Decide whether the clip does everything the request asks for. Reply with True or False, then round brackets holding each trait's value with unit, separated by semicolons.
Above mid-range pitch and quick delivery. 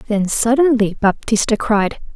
False (225 Hz; 110 wpm)